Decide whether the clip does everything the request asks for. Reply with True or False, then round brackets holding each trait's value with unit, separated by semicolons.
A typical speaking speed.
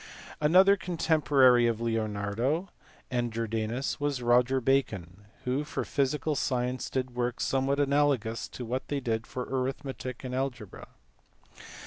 False (125 wpm)